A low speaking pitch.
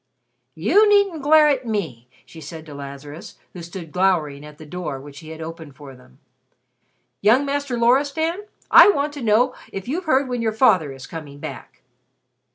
No: medium, 185 Hz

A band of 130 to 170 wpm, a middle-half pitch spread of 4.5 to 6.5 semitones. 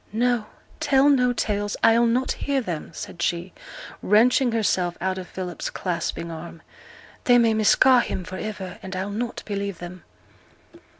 Yes: average, 155 wpm; average, 5.0 semitones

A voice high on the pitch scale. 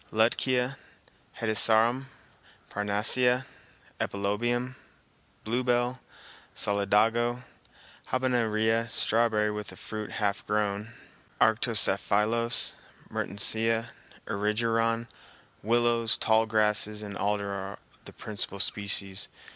No: low, 110 Hz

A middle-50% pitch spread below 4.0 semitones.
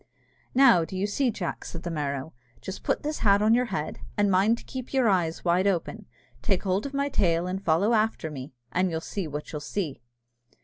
No: average, 4.8 semitones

